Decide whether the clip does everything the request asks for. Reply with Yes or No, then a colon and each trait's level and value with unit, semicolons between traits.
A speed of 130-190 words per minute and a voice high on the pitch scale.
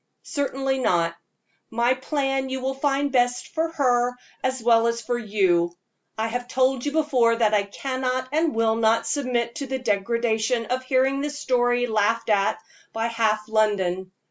Yes: average, 165 wpm; high, 245 Hz